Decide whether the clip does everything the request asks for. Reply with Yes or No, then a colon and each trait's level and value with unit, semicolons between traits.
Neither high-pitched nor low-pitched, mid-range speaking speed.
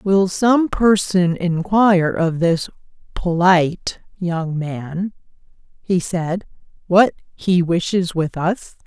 No: medium, 180 Hz; slow, 110 wpm